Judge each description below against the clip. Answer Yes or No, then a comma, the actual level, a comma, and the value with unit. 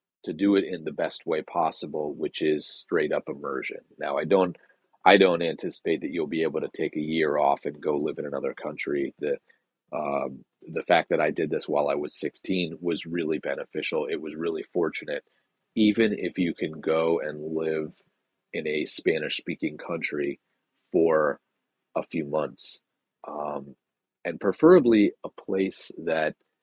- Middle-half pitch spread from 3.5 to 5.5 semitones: Yes, average, 5.0 semitones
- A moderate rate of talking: Yes, average, 170 wpm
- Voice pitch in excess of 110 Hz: No, very low, 85 Hz